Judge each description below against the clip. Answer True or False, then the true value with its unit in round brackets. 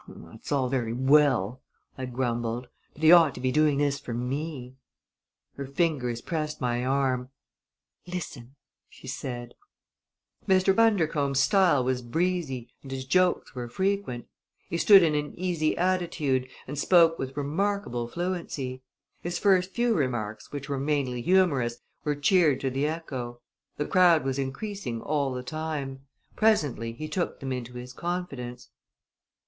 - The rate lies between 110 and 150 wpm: True (145 wpm)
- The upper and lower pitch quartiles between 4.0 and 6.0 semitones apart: True (5.1 semitones)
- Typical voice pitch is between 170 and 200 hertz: False (140 Hz)